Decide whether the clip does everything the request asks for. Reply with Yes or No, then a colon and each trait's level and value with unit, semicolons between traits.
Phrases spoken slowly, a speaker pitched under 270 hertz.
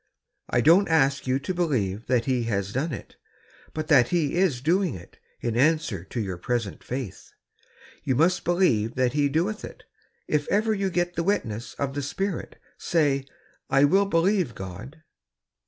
No: average, 175 wpm; medium, 140 Hz